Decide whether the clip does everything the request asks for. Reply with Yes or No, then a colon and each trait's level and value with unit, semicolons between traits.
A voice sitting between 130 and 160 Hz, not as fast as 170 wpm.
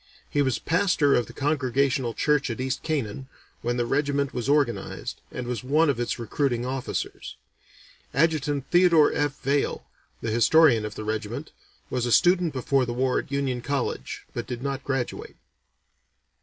Yes: low, 135 Hz; average, 160 wpm